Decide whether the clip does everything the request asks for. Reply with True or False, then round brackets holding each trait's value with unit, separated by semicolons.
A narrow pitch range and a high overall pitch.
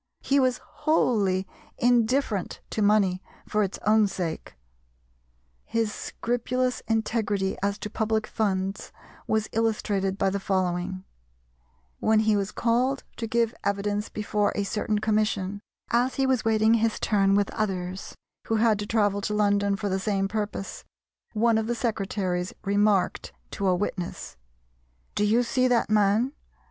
True (2.3 semitones; 210 Hz)